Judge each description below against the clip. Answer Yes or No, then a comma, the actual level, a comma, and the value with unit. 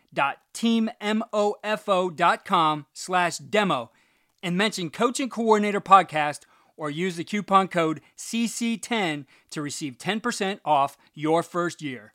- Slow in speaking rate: Yes, slow, 100 wpm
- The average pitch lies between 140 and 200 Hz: Yes, medium, 185 Hz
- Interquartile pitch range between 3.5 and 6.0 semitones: Yes, wide, 5.4 semitones